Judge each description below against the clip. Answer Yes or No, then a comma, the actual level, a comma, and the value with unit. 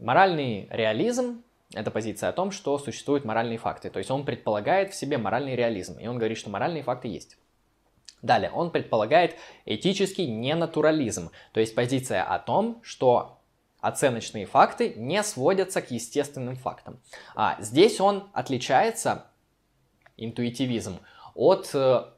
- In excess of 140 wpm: No, average, 135 wpm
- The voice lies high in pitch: No, low, 135 Hz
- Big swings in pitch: Yes, wide, 8.7 semitones